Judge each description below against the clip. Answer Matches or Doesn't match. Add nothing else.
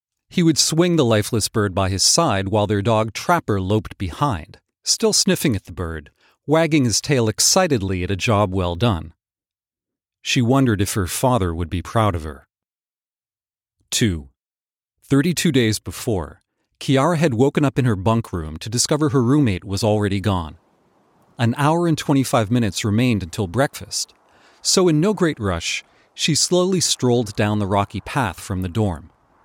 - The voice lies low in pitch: Matches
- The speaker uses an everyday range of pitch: Doesn't match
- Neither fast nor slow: Matches